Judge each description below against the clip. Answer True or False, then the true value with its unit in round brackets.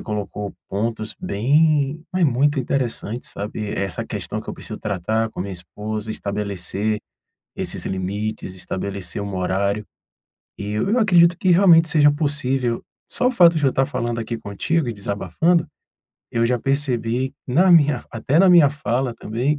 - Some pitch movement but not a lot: False (6.3 semitones)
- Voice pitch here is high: False (120 Hz)